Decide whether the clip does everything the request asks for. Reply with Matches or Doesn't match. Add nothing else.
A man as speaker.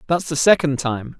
Matches